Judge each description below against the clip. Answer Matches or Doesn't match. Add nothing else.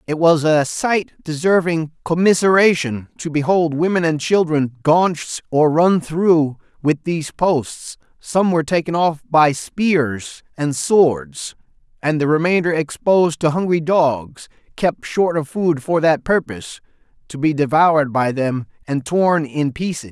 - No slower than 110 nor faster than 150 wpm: Matches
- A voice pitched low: Doesn't match